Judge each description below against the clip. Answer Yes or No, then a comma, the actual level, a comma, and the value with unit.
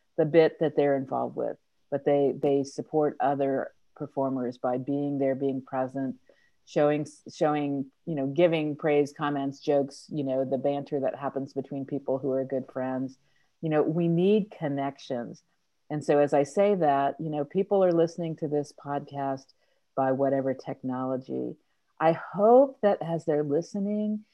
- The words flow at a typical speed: Yes, average, 160 wpm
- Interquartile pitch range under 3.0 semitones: Yes, narrow, 2.6 semitones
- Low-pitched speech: No, medium, 145 Hz